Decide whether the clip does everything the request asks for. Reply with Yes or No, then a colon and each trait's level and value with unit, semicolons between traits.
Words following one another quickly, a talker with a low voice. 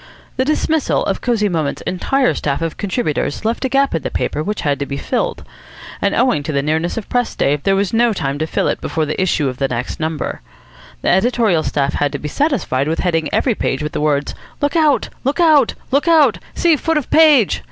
No: fast, 225 wpm; high, 190 Hz